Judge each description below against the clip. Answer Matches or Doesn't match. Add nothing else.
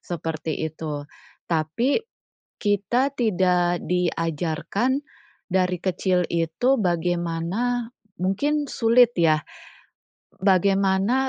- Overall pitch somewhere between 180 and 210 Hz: Matches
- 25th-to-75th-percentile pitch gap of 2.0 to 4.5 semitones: Doesn't match